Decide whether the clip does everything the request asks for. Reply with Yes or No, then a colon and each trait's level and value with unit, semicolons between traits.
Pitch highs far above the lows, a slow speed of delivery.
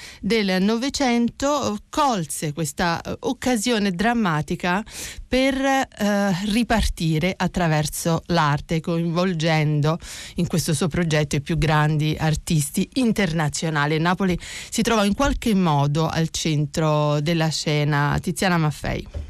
No: average, 5.0 semitones; slow, 105 wpm